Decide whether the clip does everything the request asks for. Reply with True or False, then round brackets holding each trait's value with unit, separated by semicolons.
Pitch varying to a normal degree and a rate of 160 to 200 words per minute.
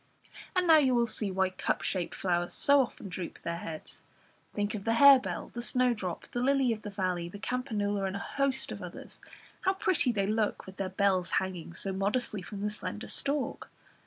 True (4.9 semitones; 195 wpm)